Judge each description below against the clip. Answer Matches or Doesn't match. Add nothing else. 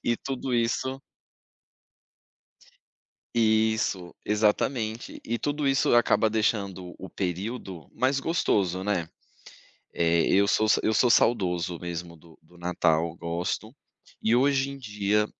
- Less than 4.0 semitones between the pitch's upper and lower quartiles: Doesn't match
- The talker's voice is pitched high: Doesn't match